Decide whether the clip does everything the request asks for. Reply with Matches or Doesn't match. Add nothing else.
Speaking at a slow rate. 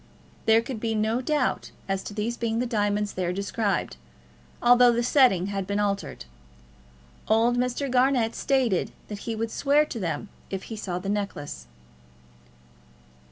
Doesn't match